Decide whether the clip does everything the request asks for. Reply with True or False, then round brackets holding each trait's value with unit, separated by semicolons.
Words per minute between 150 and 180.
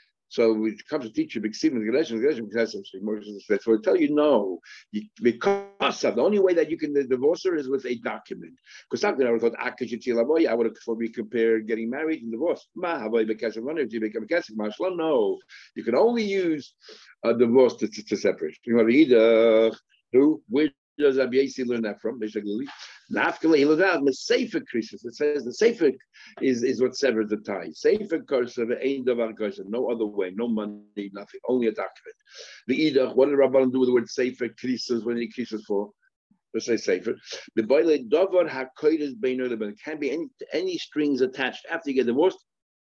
False (205 wpm)